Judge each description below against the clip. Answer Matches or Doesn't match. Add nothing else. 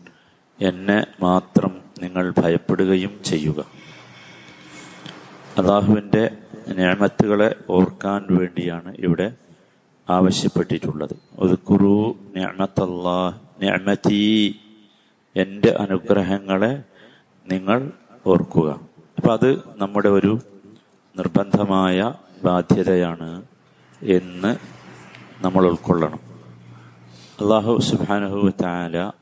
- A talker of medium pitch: Doesn't match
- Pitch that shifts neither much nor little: Doesn't match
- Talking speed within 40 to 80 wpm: Matches